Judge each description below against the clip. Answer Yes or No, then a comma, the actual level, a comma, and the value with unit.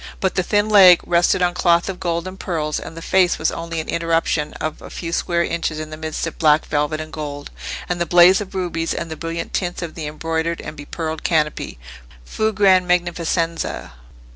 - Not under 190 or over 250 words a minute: Yes, average, 200 wpm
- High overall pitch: No, medium, 165 Hz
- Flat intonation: Yes, narrow, 2.2 semitones